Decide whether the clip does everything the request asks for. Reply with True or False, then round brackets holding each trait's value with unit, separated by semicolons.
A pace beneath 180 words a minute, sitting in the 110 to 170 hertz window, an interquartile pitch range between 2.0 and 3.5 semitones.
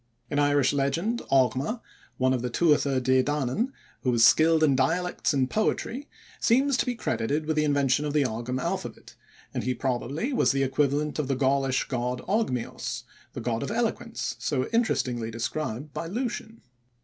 False (170 wpm; 140 Hz; 4.6 semitones)